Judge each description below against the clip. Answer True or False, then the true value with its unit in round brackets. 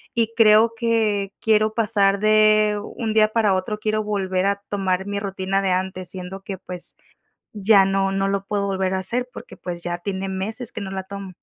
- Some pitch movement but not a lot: False (2.0 semitones)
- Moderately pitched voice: False (200 Hz)